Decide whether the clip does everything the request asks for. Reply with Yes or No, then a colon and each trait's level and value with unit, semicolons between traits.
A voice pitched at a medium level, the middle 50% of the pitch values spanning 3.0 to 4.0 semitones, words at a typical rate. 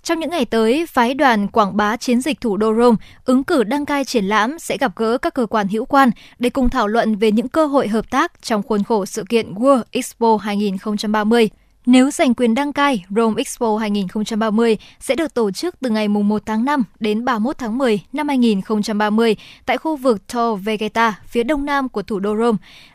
No: high, 230 Hz; average, 3.4 semitones; average, 210 wpm